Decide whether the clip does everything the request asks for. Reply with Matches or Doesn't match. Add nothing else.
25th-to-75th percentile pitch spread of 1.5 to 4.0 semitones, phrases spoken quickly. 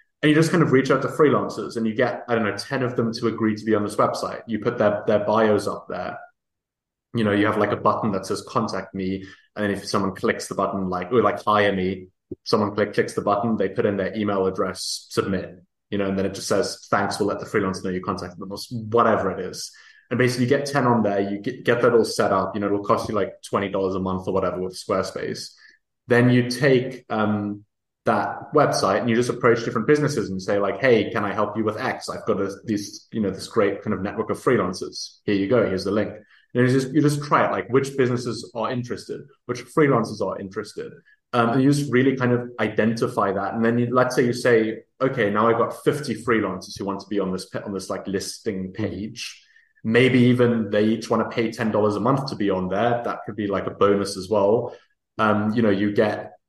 Matches